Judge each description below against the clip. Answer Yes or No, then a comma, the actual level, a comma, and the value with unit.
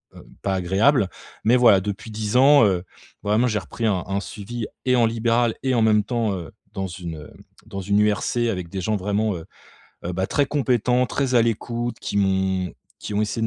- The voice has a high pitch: No, low, 105 Hz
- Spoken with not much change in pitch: No, average, 3.7 semitones